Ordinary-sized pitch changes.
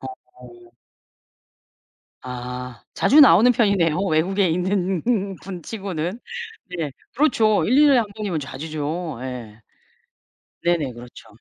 No: wide, 7.7 semitones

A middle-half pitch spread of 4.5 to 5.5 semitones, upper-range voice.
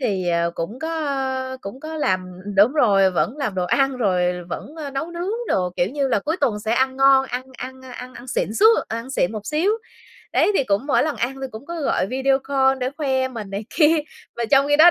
Yes: average, 5.0 semitones; very high, 260 Hz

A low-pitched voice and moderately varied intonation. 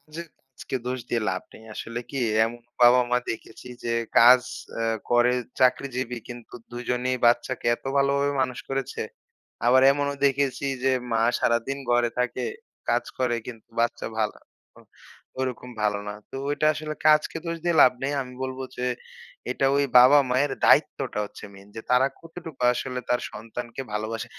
No: low, 125 Hz; narrow, 2.3 semitones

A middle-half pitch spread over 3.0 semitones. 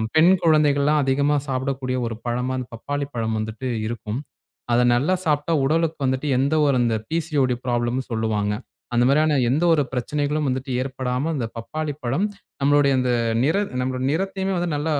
Yes: average, 3.5 semitones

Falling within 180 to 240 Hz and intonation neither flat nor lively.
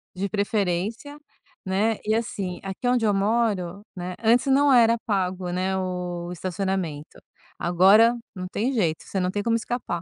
Yes: high, 195 Hz; average, 3.8 semitones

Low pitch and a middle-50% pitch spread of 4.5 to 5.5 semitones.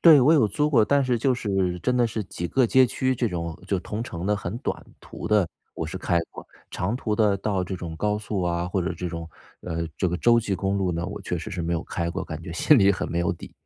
Yes: very low, 95 Hz; average, 4.8 semitones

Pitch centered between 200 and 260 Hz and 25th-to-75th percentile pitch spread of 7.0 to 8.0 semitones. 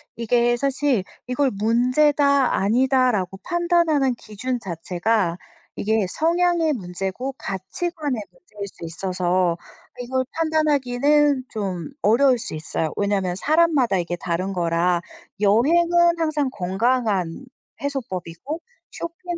Yes: high, 245 Hz; wide, 7.4 semitones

